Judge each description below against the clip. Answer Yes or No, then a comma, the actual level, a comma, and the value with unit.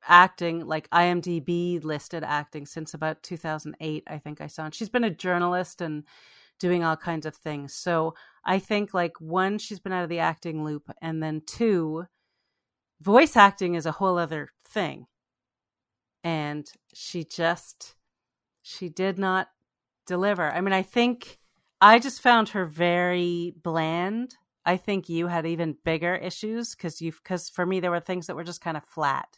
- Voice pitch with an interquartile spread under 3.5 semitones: Yes, average, 2.8 semitones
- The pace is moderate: Yes, average, 170 wpm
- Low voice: No, medium, 175 Hz